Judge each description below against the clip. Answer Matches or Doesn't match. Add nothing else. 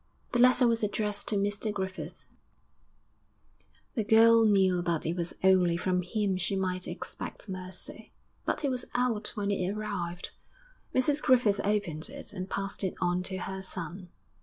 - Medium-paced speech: Matches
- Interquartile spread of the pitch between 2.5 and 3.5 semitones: Matches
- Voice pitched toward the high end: Matches